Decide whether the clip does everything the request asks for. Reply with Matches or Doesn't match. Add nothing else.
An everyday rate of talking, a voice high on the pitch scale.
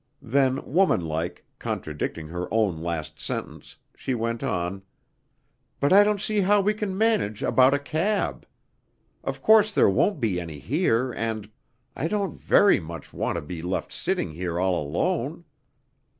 Doesn't match